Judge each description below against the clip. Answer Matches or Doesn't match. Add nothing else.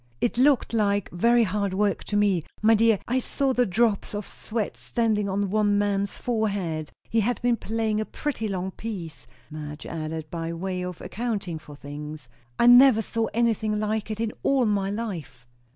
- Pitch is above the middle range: Matches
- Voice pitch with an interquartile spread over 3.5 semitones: Matches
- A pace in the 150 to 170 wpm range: Doesn't match